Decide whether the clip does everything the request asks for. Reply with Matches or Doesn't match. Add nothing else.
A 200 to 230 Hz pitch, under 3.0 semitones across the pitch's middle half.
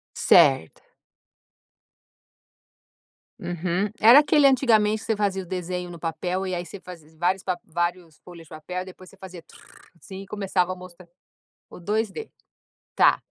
Doesn't match